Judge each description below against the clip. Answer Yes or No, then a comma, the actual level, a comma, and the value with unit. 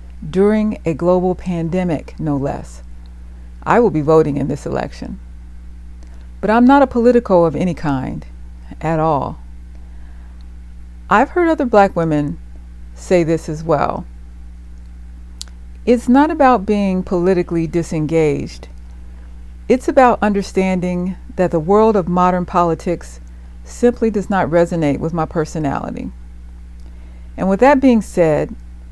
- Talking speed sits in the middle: No, slow, 120 wpm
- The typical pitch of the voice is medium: Yes, medium, 155 Hz